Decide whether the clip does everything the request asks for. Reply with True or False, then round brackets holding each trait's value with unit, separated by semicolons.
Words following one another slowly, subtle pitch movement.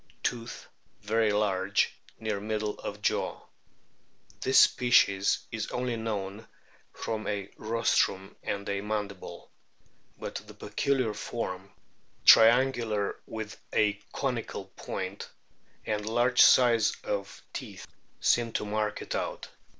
True (110 wpm; 2.3 semitones)